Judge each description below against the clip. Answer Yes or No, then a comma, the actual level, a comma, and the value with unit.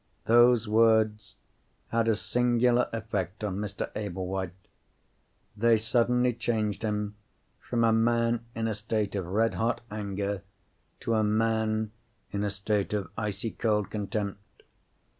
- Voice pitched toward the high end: No, low, 110 Hz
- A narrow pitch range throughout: Yes, narrow, 2.0 semitones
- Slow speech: Yes, slow, 130 wpm